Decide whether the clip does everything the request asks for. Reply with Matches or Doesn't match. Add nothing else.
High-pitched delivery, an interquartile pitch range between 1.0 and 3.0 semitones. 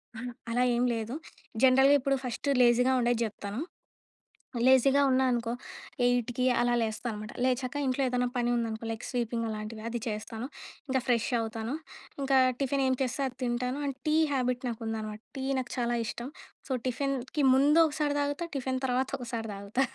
Matches